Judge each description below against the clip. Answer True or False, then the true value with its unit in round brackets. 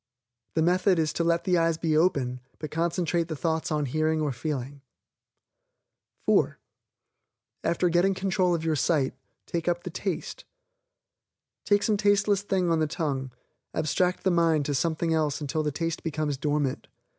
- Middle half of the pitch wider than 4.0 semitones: False (2.7 semitones)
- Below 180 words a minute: True (160 wpm)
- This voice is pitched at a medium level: True (165 Hz)